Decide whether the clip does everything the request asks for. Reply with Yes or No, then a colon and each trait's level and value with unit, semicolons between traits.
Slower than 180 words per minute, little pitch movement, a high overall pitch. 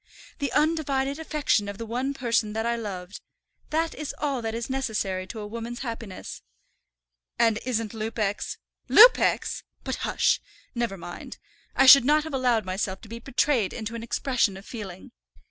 No: average, 165 wpm; average, 4.2 semitones; high, 230 Hz